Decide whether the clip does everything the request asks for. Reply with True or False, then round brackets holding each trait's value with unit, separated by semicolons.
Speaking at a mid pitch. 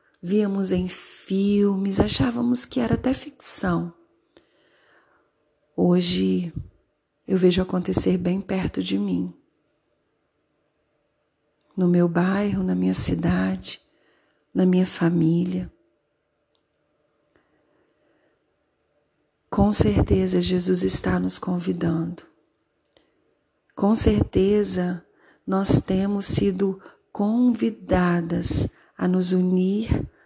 True (175 Hz)